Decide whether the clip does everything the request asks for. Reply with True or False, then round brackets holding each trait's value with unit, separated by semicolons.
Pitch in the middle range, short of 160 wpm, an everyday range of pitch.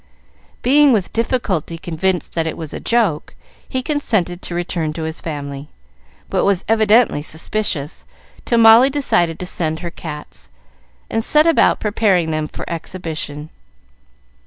False (175 Hz; 140 wpm; 5.9 semitones)